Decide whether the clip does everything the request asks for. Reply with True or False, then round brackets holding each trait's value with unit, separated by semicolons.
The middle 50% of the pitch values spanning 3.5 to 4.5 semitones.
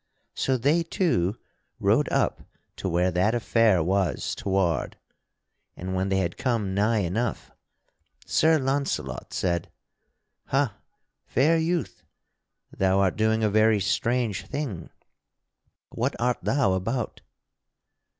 False (5.2 semitones)